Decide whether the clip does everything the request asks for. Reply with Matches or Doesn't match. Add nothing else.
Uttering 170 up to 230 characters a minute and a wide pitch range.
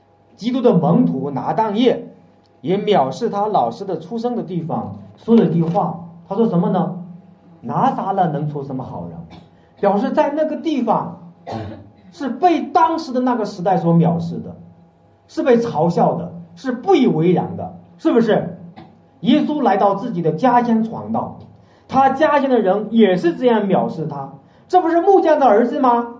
Doesn't match